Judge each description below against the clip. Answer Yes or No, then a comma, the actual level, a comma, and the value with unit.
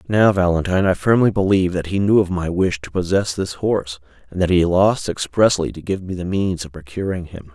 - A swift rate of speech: Yes, fast, 225 wpm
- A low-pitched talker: Yes, very low, 90 Hz